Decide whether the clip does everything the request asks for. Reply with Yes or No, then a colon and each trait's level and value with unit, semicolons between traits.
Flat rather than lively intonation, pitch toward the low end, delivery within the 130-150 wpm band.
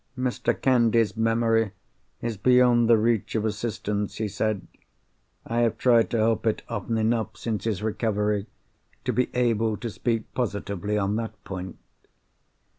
Yes: narrow, 2.0 semitones; low, 110 Hz; average, 145 wpm